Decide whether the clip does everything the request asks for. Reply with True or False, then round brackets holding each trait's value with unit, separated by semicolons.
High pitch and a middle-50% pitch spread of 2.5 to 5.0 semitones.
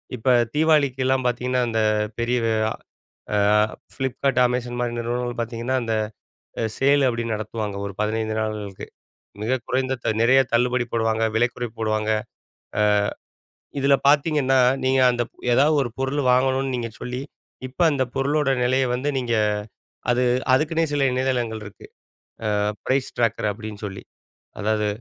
False (125 Hz; 2.9 semitones)